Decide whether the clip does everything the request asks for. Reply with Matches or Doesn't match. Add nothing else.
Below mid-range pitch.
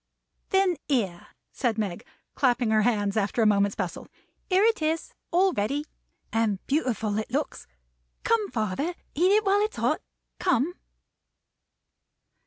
Doesn't match